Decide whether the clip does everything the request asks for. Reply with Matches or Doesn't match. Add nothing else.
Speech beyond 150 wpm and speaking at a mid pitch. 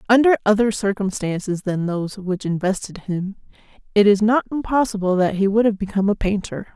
Doesn't match